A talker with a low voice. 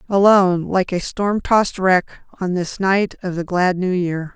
No: medium, 185 Hz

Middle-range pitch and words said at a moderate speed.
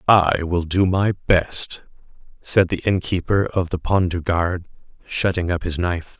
No: very low, 90 Hz; average, 175 wpm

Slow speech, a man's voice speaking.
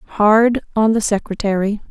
No: slow, 125 wpm; female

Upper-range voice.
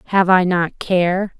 No: medium, 180 Hz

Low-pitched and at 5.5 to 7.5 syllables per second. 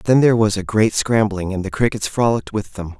Yes: low, 105 Hz; 6.0 syllables/s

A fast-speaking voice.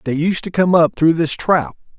Yes: fast, 240 wpm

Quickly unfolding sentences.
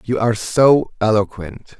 No: slow, 135 wpm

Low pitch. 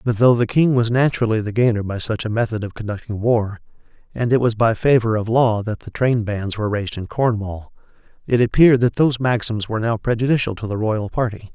Yes: low, 115 Hz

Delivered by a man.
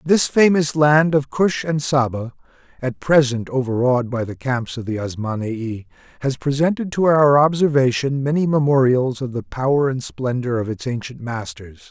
Yes: male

